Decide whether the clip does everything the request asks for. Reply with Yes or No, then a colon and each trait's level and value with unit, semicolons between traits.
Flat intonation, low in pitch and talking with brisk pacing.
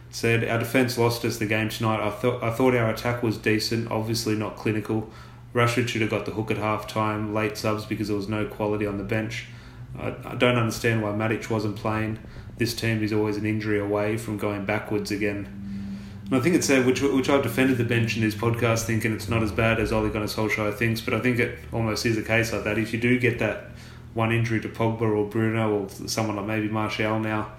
Yes: narrow, 1.5 semitones; low, 110 Hz; fast, 235 wpm